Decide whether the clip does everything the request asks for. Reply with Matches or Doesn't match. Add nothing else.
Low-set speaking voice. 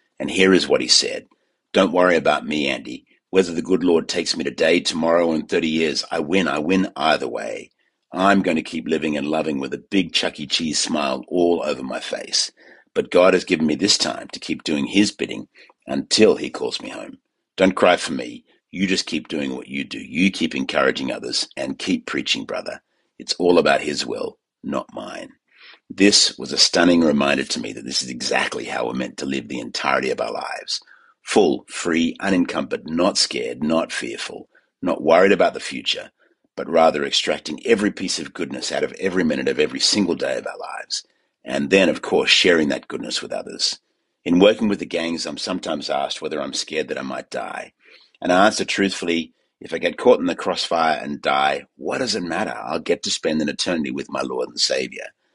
Matches